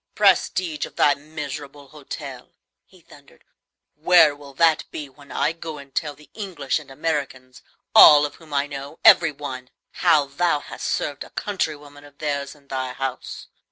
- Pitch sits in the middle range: Yes, medium, 145 Hz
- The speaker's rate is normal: Yes, average, 165 wpm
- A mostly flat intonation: Yes, narrow, 2.1 semitones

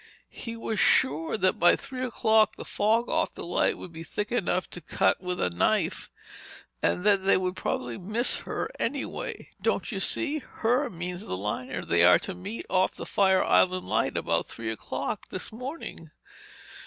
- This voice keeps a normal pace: Yes, average, 170 wpm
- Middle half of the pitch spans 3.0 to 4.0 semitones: No, average, 5.2 semitones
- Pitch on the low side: No, medium, 185 Hz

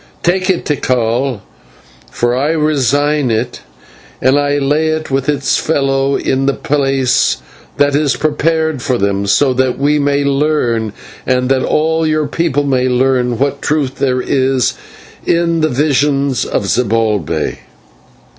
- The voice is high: No, medium, 140 Hz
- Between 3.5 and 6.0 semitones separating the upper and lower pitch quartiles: No, average, 2.8 semitones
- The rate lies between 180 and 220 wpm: No, slow, 135 wpm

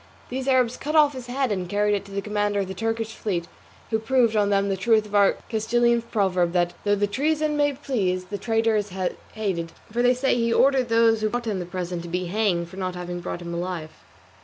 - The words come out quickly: Yes, fast, 235 wpm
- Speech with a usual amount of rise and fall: Yes, average, 4.4 semitones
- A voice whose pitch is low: No, high, 210 Hz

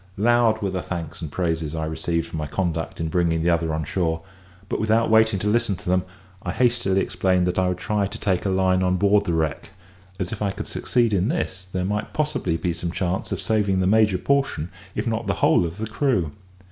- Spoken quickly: Yes, fast, 230 wpm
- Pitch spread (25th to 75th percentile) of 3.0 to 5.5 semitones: Yes, average, 3.8 semitones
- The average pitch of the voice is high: No, very low, 95 Hz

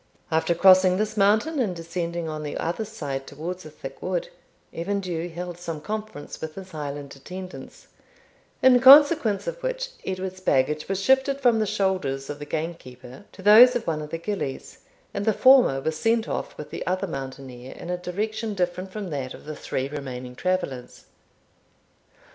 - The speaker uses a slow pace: No, average, 175 wpm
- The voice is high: No, medium, 180 Hz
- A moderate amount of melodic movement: No, wide, 5.9 semitones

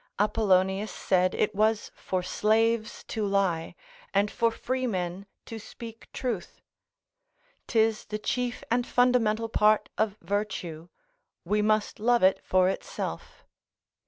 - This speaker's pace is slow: Yes, slow, 120 wpm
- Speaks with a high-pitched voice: Yes, high, 210 Hz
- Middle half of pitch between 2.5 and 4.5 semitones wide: Yes, average, 2.9 semitones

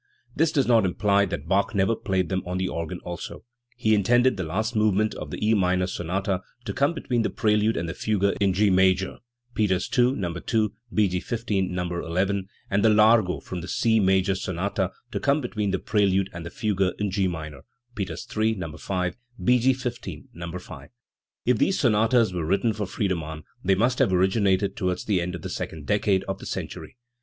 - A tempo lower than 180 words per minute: No, fast, 205 wpm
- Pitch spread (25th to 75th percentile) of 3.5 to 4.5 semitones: No, average, 3.1 semitones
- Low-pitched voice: Yes, very low, 95 Hz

